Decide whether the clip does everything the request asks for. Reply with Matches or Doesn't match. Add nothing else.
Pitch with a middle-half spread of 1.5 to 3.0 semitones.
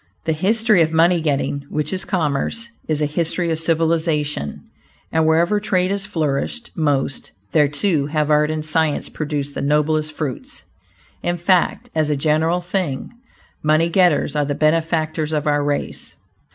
Matches